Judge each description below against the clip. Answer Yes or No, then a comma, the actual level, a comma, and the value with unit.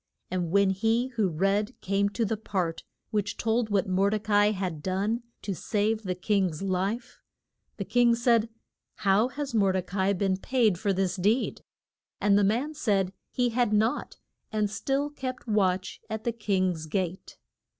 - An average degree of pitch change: Yes, average, 3.1 semitones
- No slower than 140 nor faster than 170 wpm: No, average, 180 wpm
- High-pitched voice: Yes, high, 205 Hz